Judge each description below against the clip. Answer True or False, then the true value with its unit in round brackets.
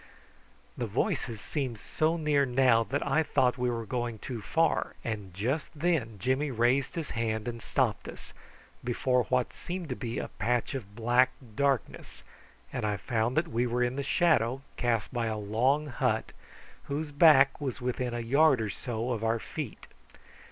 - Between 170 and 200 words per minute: True (175 wpm)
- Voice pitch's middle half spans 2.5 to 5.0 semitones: True (3.5 semitones)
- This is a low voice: True (125 Hz)